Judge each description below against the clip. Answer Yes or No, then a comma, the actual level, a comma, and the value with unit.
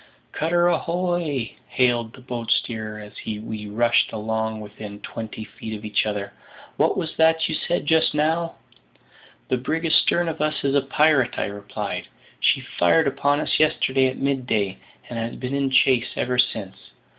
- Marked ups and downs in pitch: Yes, wide, 5.8 semitones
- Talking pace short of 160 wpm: No, average, 170 wpm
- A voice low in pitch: Yes, low, 125 Hz